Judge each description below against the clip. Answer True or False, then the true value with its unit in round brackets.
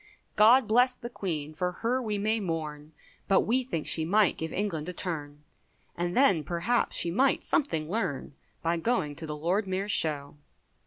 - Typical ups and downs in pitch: False (5.9 semitones)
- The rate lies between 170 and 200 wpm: True (175 wpm)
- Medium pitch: True (180 Hz)